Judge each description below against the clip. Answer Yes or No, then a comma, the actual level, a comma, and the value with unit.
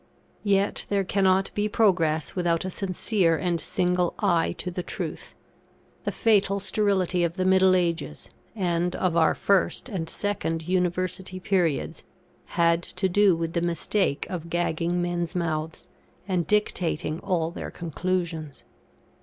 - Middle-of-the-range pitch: Yes, medium, 180 Hz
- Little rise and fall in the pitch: Yes, narrow, 2.2 semitones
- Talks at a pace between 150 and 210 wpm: No, slow, 135 wpm